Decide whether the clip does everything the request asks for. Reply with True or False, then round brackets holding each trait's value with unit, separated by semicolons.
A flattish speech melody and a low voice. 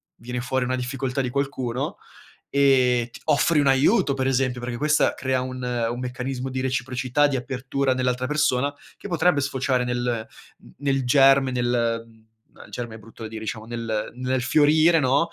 True (2.0 semitones; 130 Hz)